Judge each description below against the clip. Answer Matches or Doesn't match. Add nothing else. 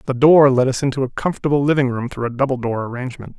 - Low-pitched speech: Matches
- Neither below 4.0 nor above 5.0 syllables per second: Doesn't match